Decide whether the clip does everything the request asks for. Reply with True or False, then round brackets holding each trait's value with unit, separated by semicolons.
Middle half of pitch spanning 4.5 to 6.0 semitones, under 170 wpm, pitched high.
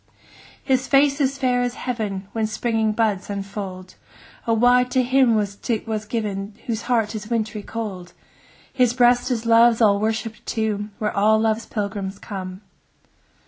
False (2.9 semitones; 155 wpm; 220 Hz)